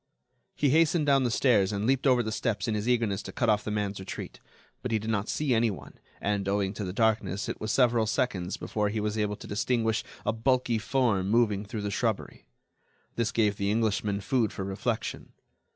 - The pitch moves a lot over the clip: No, average, 2.8 semitones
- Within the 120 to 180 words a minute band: No, fast, 205 wpm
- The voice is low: Yes, low, 110 Hz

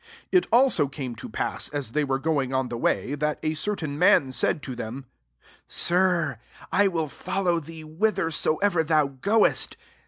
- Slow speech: No, average, 180 wpm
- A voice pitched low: No, medium, 155 Hz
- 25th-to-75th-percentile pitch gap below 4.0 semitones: No, average, 4.7 semitones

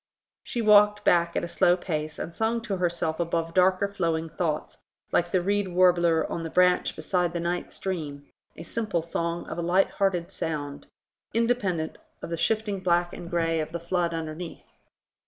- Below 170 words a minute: No, average, 175 wpm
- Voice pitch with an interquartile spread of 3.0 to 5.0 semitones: No, narrow, 2.4 semitones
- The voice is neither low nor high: Yes, medium, 175 Hz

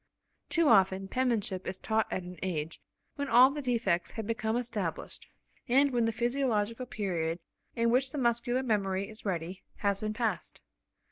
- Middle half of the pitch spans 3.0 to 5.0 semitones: Yes, average, 4.4 semitones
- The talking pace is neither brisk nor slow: Yes, average, 160 wpm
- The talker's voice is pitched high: Yes, high, 220 Hz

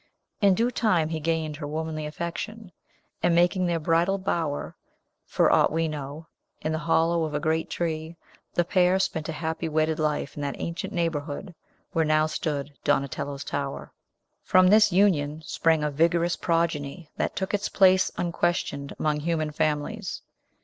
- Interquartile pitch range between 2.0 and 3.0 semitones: Yes, narrow, 2.4 semitones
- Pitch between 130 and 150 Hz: No, medium, 160 Hz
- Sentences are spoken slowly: No, average, 160 wpm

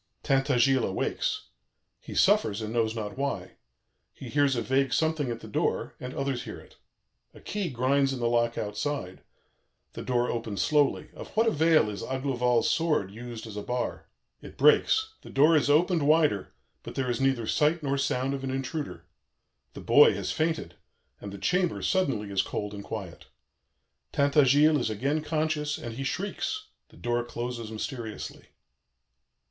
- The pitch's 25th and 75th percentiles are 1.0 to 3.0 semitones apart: No, average, 4.3 semitones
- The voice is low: Yes, low, 130 Hz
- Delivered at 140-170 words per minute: Yes, average, 165 wpm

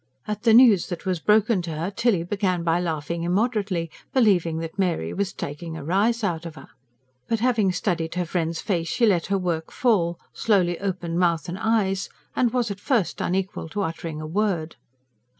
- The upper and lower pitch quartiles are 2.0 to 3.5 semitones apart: No, average, 3.9 semitones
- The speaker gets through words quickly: No, average, 185 wpm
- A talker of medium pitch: Yes, medium, 180 Hz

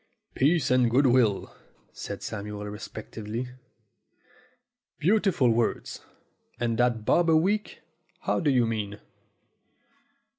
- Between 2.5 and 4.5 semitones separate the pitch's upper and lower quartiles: No, average, 5.1 semitones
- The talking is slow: Yes, slow, 105 wpm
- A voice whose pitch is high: No, low, 120 Hz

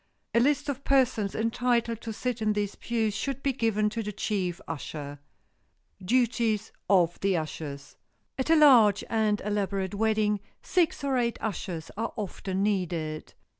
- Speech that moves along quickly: No, average, 160 wpm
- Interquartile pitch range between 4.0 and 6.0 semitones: No, average, 3.6 semitones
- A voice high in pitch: Yes, high, 215 Hz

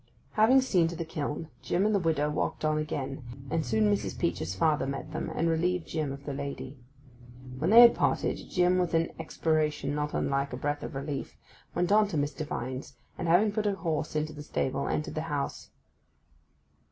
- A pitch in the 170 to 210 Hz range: No, medium, 155 Hz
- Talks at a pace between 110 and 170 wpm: No, average, 195 wpm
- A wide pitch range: No, average, 3.7 semitones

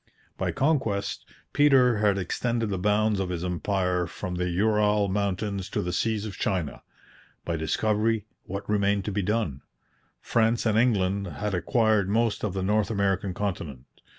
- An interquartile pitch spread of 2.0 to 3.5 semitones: Yes, average, 2.9 semitones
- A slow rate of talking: No, average, 155 wpm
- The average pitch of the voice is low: Yes, low, 100 Hz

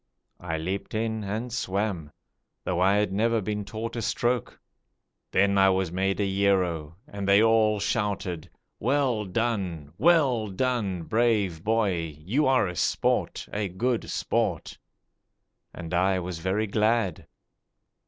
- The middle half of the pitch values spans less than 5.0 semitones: Yes, average, 3.5 semitones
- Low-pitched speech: Yes, low, 100 Hz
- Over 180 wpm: No, slow, 135 wpm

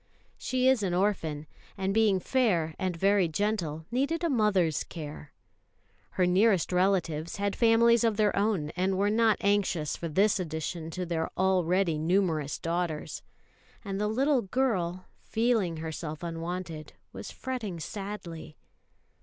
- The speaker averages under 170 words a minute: Yes, slow, 135 wpm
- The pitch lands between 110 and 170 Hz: No, medium, 185 Hz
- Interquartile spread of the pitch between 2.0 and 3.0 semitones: No, average, 4.3 semitones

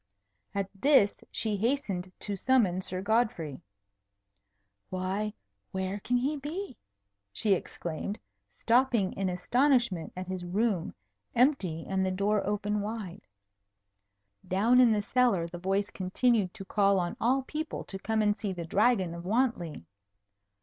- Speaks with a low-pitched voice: No, high, 200 Hz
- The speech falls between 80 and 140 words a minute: Yes, slow, 135 wpm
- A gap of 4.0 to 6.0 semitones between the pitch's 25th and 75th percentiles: Yes, average, 4.3 semitones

